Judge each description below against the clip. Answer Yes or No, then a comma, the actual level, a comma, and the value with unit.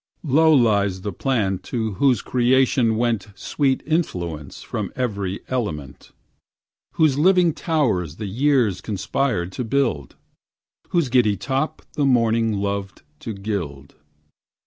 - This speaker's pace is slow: Yes, slow, 120 wpm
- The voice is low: Yes, low, 115 Hz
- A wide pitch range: Yes, wide, 5.7 semitones